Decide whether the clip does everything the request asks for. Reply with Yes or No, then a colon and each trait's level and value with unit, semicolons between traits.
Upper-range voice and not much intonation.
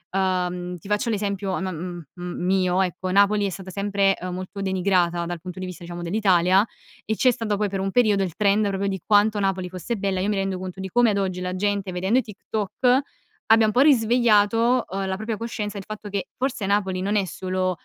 Yes: high, 195 Hz; narrow, 2.2 semitones